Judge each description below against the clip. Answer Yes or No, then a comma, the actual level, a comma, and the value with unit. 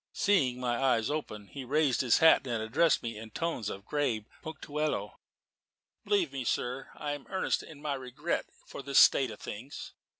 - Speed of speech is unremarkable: Yes, average, 175 wpm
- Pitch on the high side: No, low, 135 Hz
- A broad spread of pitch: No, average, 4.2 semitones